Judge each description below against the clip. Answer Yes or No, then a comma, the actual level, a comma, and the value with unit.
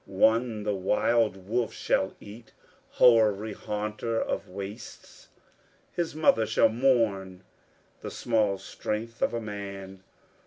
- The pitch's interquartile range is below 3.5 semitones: Yes, average, 2.7 semitones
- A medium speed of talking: No, slow, 115 wpm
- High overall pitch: No, low, 105 Hz